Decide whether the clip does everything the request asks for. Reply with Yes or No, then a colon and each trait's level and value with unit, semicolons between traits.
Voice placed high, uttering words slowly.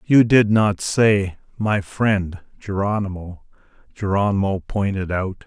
No: low, 100 Hz; slow, 110 wpm